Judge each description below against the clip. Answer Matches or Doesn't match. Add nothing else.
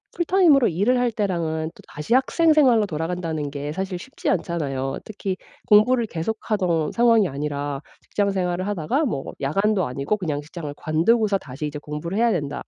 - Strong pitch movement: Matches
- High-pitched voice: Doesn't match